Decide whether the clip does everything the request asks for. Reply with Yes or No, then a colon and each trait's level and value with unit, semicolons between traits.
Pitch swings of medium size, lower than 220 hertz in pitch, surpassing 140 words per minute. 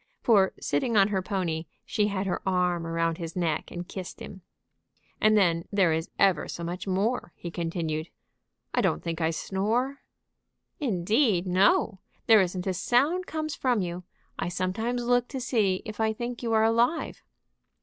Yes: average, 4.6 semitones; high, 190 Hz; average, 170 wpm